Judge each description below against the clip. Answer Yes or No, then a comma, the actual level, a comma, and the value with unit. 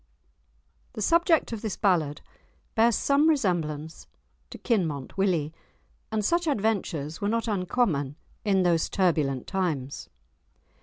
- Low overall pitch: No, high, 190 Hz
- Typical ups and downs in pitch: No, wide, 6.4 semitones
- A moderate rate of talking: No, slow, 115 wpm